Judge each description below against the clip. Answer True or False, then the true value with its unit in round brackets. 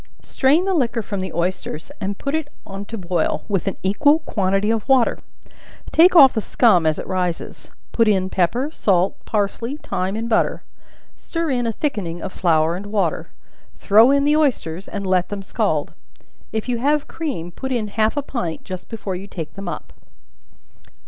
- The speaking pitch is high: True (205 Hz)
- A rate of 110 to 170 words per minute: False (180 wpm)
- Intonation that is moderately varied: False (6.0 semitones)